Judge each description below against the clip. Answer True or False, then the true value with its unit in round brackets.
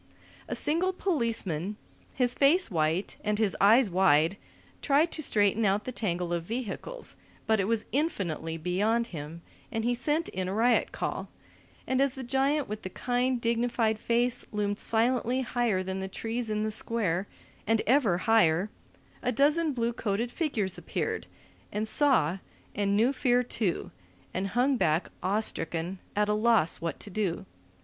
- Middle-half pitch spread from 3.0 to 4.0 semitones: False (4.6 semitones)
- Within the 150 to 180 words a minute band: True (160 wpm)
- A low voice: False (220 Hz)